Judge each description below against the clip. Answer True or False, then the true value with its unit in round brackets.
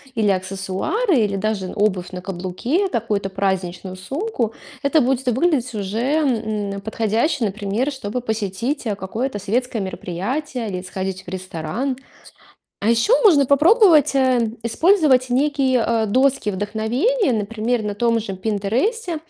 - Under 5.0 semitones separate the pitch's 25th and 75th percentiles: False (5.3 semitones)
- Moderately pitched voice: False (225 Hz)